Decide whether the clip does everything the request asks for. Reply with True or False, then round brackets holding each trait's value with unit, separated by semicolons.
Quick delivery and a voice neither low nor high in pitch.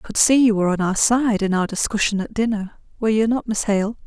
False (250 wpm; 215 Hz)